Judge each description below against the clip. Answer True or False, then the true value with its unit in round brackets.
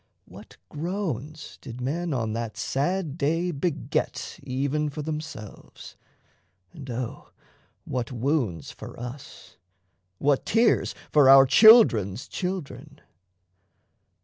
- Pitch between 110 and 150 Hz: True (140 Hz)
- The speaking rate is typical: False (100 wpm)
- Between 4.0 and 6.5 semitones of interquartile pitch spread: True (4.9 semitones)